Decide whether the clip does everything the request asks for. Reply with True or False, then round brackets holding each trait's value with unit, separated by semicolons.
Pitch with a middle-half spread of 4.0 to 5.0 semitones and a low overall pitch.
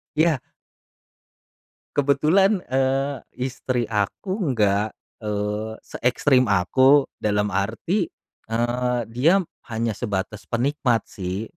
True (4.6 semitones; 120 Hz)